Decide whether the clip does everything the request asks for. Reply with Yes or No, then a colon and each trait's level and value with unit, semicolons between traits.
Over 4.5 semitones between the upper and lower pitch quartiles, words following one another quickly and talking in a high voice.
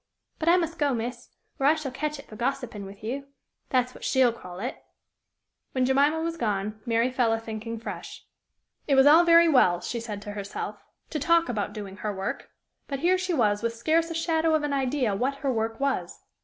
Yes: average, 5.3 semitones; fast, 210 wpm; very high, 255 Hz